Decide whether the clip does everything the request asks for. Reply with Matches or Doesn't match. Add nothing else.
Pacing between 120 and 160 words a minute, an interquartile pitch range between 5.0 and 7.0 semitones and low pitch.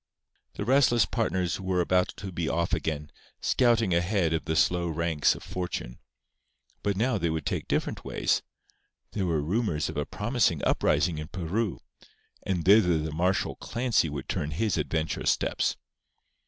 Doesn't match